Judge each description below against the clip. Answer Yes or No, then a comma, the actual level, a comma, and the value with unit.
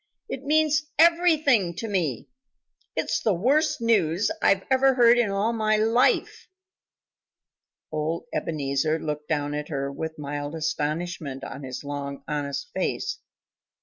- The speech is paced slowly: Yes, slow, 130 wpm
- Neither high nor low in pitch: Yes, medium, 170 Hz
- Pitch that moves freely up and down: Yes, wide, 8.3 semitones